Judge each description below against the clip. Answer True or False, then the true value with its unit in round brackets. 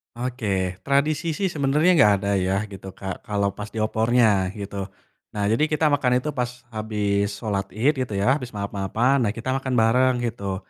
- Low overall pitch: True (110 Hz)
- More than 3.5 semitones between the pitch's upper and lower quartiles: True (4.4 semitones)